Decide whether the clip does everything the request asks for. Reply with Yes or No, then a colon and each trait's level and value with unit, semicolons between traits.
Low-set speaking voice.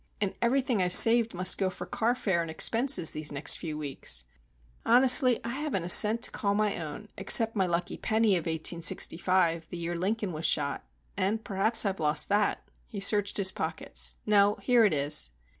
No: high, 195 Hz